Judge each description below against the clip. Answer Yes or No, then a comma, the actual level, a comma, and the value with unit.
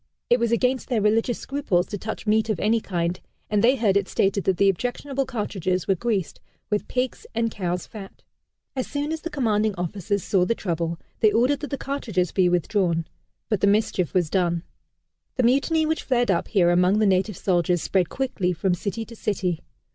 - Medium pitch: No, high, 205 Hz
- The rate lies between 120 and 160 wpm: No, average, 195 wpm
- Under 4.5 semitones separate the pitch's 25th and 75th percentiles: No, average, 4.8 semitones